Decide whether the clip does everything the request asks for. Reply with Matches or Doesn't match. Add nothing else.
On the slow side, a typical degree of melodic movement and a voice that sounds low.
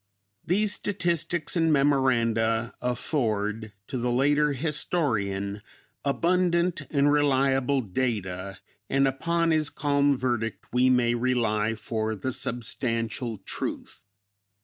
Matches